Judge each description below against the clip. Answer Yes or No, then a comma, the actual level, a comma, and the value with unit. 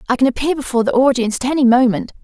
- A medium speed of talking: No, fast, 240 wpm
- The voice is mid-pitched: No, very high, 250 Hz